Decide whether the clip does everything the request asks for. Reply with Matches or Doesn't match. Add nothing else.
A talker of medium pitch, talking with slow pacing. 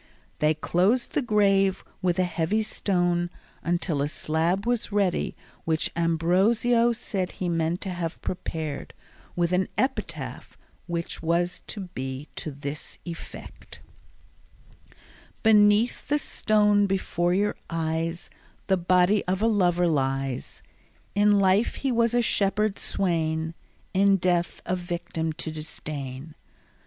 Matches